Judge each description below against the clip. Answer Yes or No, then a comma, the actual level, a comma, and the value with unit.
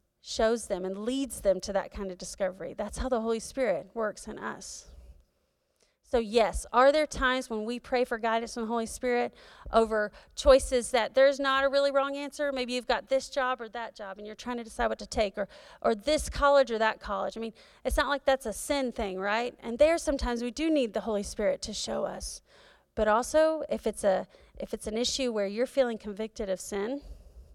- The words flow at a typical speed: No, fast, 220 wpm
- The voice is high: Yes, high, 235 Hz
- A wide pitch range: No, average, 4.0 semitones